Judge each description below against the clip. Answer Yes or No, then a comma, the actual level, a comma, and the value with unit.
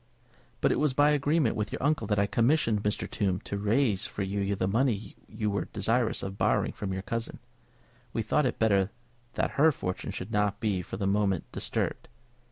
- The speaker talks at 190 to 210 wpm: Yes, average, 195 wpm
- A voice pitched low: Yes, low, 105 Hz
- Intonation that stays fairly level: No, average, 3.3 semitones